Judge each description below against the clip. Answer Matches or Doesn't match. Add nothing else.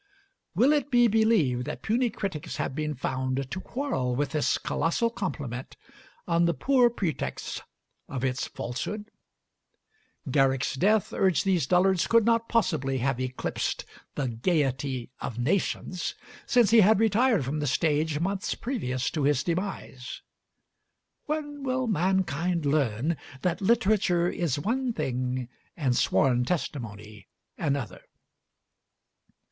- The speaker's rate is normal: Doesn't match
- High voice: Doesn't match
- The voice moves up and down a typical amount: Doesn't match